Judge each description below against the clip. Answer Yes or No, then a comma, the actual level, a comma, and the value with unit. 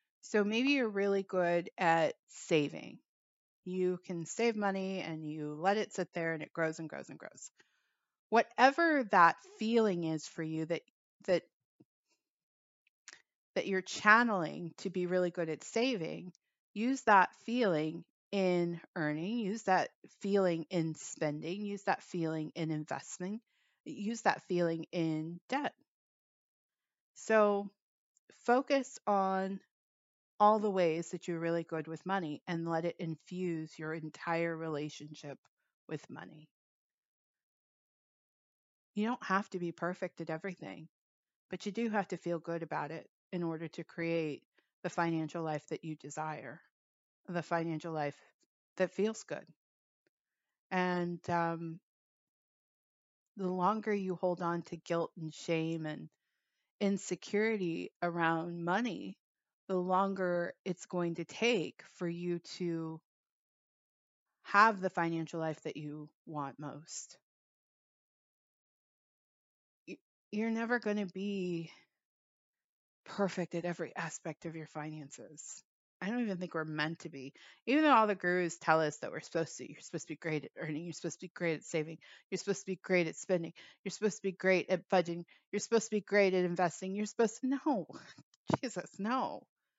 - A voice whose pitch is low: No, medium, 175 Hz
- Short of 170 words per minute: Yes, average, 150 wpm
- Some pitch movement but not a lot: Yes, average, 3.6 semitones